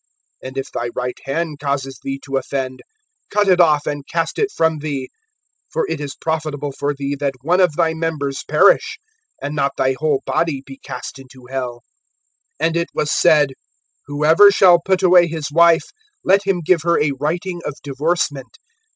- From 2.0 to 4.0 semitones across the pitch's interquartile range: Yes, average, 3.6 semitones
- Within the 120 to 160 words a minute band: No, average, 175 wpm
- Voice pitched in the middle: Yes, medium, 150 Hz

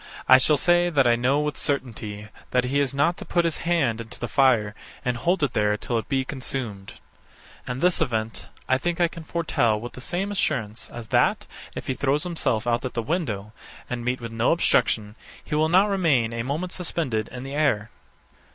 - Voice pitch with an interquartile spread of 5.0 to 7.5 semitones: Yes, wide, 5.6 semitones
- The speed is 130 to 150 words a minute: No, fast, 205 wpm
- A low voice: Yes, low, 130 Hz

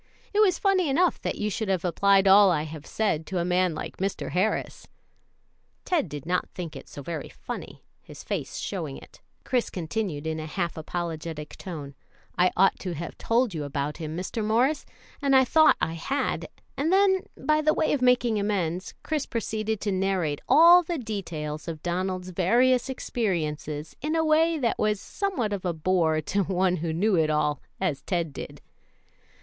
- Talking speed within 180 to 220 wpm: Yes, average, 185 wpm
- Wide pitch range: Yes, wide, 7.2 semitones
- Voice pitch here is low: No, high, 190 Hz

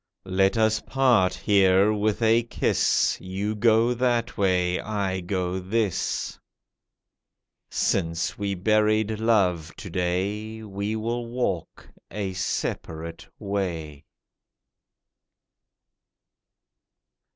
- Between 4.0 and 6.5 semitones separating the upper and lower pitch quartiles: No, average, 3.1 semitones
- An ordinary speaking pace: No, slow, 90 wpm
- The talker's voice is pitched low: Yes, low, 100 Hz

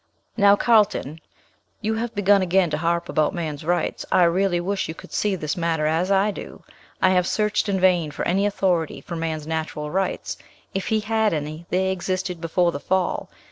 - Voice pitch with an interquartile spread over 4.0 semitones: No, average, 3.3 semitones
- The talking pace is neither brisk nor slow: Yes, average, 190 wpm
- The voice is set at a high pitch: No, medium, 180 Hz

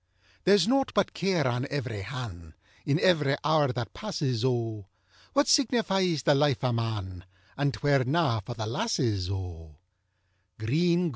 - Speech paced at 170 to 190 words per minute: No, average, 140 wpm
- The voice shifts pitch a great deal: Yes, wide, 6.9 semitones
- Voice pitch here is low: Yes, low, 130 Hz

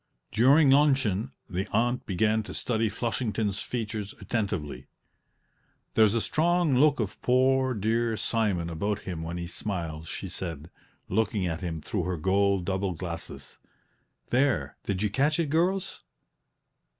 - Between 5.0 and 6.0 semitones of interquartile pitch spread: Yes, wide, 5.6 semitones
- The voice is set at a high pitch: No, low, 105 Hz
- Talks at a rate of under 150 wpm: Yes, average, 140 wpm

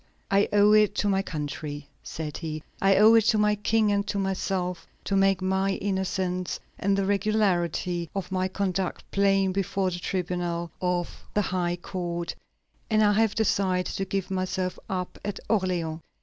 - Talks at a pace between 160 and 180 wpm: Yes, average, 165 wpm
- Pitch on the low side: No, high, 190 Hz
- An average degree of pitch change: No, narrow, 2.1 semitones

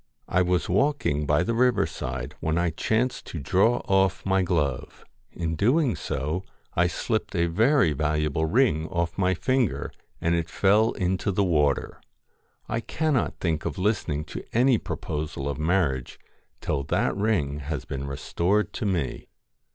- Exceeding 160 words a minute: No, average, 155 wpm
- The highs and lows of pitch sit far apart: Yes, wide, 5.7 semitones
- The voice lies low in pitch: Yes, very low, 90 Hz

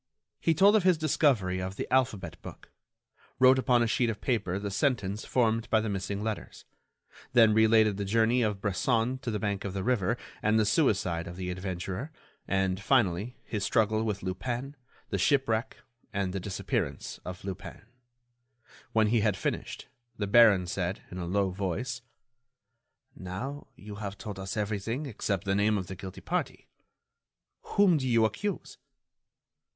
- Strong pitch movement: No, average, 3.9 semitones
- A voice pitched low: Yes, low, 105 Hz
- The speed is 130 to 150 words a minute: No, average, 165 wpm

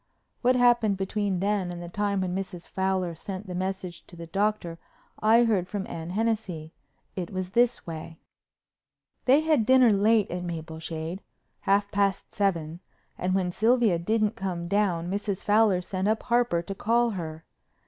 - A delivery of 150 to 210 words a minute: Yes, average, 155 wpm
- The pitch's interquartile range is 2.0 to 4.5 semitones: Yes, average, 3.5 semitones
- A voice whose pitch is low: No, high, 195 Hz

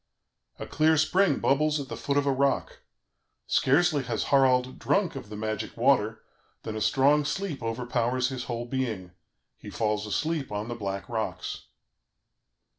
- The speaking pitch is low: Yes, low, 130 Hz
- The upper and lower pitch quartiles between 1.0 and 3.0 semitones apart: No, average, 4.3 semitones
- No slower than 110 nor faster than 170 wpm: Yes, average, 155 wpm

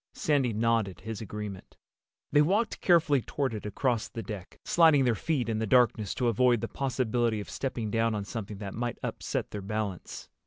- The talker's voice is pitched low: Yes, low, 115 Hz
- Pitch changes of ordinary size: Yes, average, 3.5 semitones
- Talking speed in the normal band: Yes, average, 185 wpm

